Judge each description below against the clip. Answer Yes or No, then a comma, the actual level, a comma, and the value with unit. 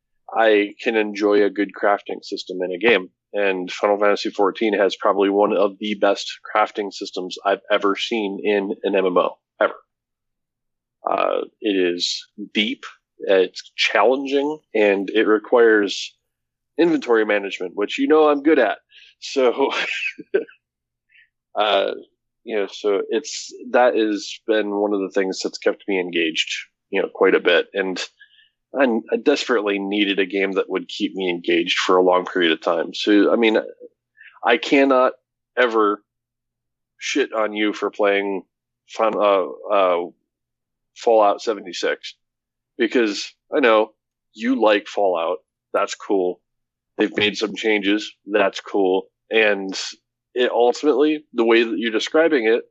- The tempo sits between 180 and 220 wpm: No, average, 140 wpm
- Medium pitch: No, low, 110 Hz